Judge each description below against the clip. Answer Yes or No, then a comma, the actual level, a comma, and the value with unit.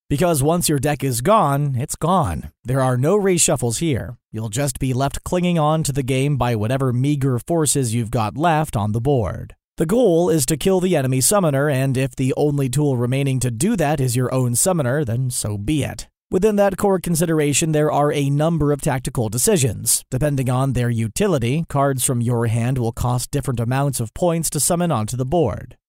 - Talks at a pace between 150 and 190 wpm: No, average, 200 wpm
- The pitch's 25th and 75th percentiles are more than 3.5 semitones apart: Yes, average, 4.1 semitones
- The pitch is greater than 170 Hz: No, medium, 140 Hz